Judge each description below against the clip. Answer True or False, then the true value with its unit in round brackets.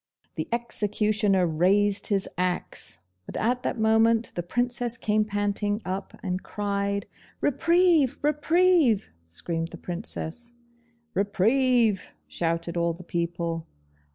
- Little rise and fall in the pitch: False (4.8 semitones)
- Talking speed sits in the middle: False (110 wpm)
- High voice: True (205 Hz)